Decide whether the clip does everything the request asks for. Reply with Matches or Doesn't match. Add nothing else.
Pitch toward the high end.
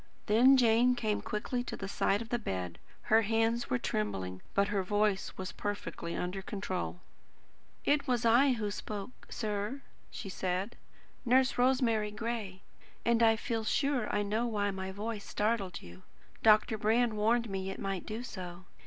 Matches